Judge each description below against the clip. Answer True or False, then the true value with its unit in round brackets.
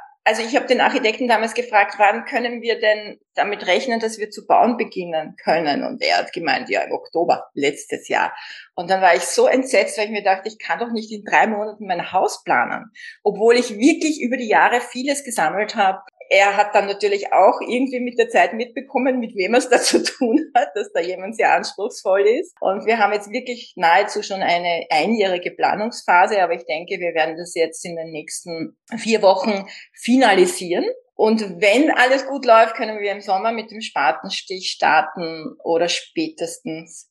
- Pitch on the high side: True (215 Hz)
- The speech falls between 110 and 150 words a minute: False (190 wpm)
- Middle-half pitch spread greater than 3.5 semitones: True (4.7 semitones)